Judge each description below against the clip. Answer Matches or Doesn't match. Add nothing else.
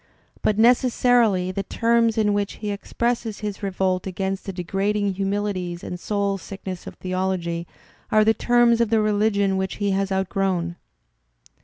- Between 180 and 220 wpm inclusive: Doesn't match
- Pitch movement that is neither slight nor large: Doesn't match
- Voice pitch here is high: Matches